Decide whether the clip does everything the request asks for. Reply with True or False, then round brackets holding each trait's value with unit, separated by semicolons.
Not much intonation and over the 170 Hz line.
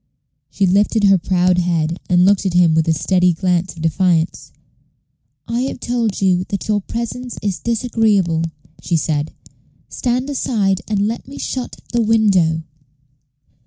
False (4.3 semitones; 190 Hz)